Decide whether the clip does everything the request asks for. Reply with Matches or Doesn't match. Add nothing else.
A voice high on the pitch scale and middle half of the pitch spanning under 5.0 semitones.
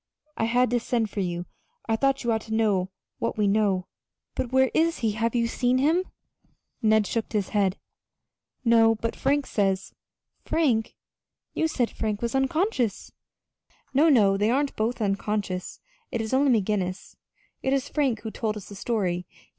Matches